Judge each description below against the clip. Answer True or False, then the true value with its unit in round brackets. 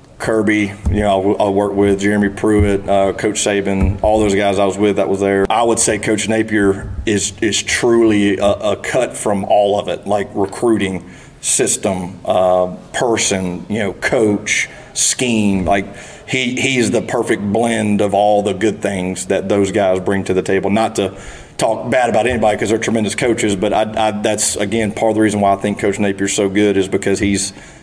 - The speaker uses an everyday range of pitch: False (1.8 semitones)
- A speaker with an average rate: True (195 wpm)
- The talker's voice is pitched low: True (100 Hz)